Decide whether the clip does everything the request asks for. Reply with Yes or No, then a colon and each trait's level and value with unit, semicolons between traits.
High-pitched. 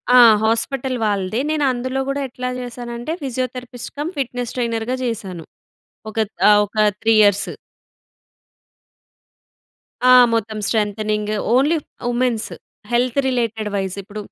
Yes: high, 235 Hz